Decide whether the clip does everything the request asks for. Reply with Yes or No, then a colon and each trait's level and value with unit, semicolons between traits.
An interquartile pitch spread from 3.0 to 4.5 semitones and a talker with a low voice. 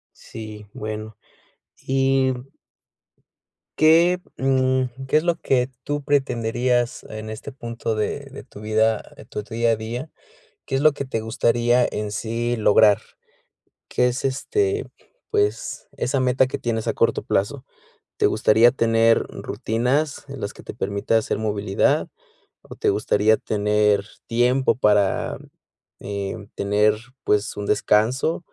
Yes: average, 3.7 semitones; low, 115 Hz